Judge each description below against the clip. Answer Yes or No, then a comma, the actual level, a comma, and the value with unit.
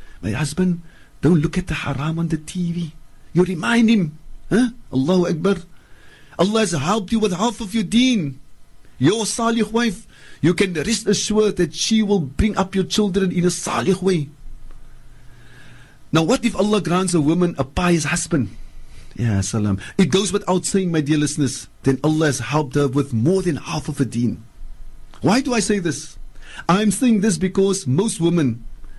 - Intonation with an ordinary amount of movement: No, wide, 5.9 semitones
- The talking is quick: No, average, 175 wpm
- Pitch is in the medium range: Yes, medium, 170 Hz